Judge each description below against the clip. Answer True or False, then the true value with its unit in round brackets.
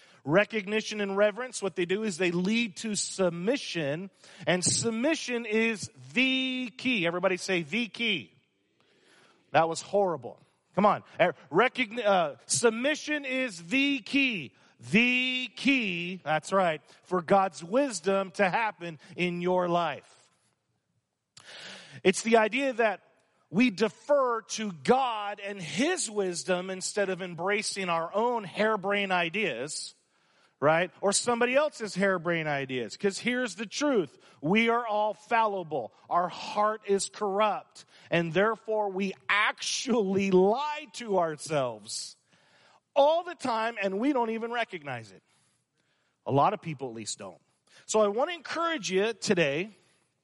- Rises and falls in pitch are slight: False (4.6 semitones)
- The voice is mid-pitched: False (205 Hz)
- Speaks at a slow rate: True (130 wpm)